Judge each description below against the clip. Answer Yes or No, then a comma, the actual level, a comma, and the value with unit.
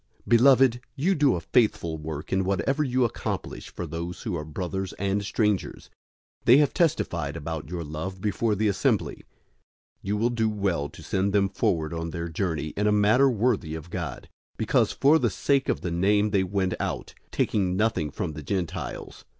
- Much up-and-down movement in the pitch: No, average, 5.0 semitones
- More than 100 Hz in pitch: No, very low, 95 Hz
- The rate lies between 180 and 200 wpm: Yes, average, 190 wpm